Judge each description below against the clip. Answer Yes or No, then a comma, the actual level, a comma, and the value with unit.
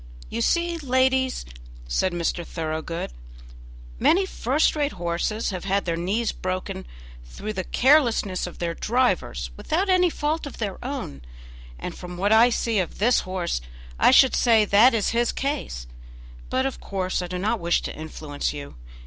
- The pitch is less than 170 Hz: No, high, 205 Hz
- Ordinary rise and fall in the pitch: No, wide, 7.0 semitones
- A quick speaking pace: No, average, 165 wpm